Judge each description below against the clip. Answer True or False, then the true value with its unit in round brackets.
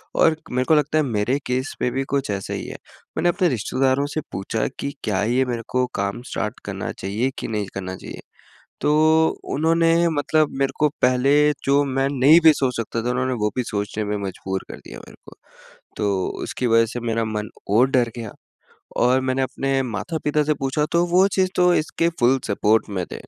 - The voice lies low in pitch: True (130 Hz)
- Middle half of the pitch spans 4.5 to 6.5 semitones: True (5.3 semitones)